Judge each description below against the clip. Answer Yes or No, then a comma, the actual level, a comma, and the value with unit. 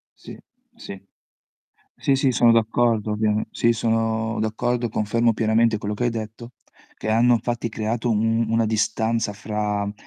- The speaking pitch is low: Yes, low, 115 Hz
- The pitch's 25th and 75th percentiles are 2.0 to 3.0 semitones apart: No, narrow, 1.4 semitones